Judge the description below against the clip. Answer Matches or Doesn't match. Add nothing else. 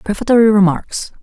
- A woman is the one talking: Doesn't match